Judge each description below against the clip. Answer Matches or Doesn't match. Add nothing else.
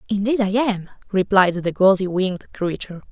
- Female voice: Matches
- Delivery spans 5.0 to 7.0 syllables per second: Matches